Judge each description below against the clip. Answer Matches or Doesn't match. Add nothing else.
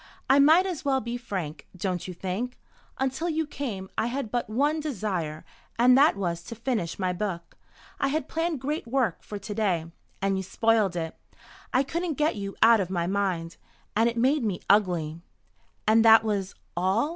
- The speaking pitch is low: Doesn't match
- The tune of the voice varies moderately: Doesn't match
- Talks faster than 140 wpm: Matches